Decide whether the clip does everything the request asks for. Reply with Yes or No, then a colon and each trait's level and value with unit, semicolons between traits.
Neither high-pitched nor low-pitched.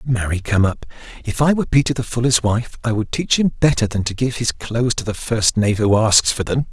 No: low, 115 Hz